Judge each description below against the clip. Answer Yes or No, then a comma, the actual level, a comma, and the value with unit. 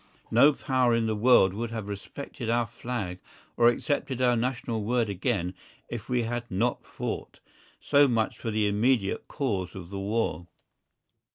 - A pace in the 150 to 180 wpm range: Yes, average, 160 wpm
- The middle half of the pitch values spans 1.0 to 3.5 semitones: Yes, average, 3.2 semitones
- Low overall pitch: Yes, low, 115 Hz